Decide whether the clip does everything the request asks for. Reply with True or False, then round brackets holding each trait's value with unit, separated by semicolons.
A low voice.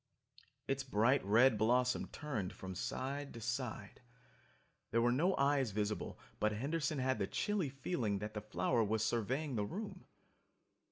True (125 Hz)